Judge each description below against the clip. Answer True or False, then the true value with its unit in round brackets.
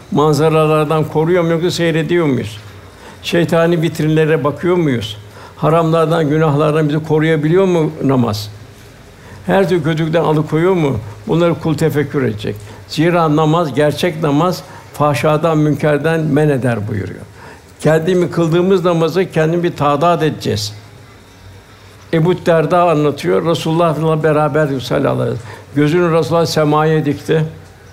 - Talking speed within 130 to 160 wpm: False (115 wpm)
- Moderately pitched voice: True (155 Hz)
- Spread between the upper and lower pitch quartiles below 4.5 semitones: False (5.0 semitones)